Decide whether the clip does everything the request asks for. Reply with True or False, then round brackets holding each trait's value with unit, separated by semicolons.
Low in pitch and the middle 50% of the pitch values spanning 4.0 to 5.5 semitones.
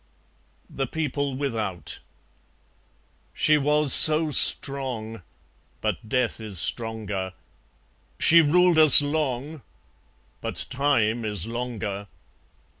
True (130 Hz; 5.2 semitones)